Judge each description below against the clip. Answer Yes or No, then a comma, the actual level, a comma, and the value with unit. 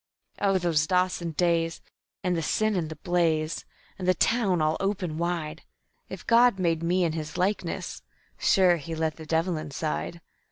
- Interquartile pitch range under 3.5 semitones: Yes, narrow, 2.5 semitones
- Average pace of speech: Yes, average, 165 wpm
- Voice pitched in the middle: Yes, medium, 170 Hz